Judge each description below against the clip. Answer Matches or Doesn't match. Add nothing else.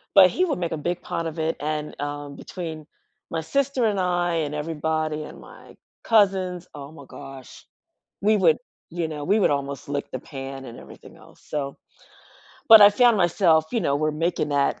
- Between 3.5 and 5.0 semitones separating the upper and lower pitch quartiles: Matches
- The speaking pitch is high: Doesn't match